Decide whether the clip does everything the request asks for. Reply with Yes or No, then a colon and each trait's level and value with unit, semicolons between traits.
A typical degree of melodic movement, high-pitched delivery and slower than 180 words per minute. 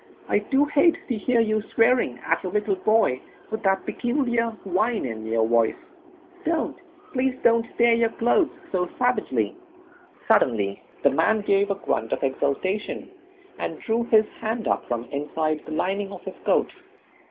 No: wide, 7.1 semitones; high, 215 Hz; average, 160 wpm